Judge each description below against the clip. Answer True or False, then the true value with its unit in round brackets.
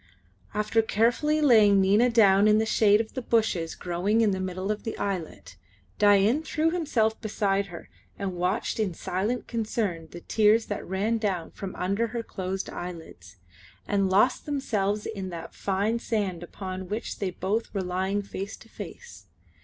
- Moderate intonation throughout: True (3.1 semitones)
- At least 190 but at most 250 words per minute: False (165 wpm)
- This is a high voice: True (205 Hz)